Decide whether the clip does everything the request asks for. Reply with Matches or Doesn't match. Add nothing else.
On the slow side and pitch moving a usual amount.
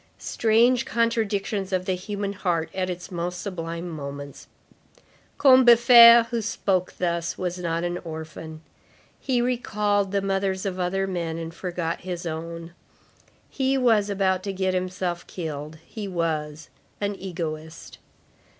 Matches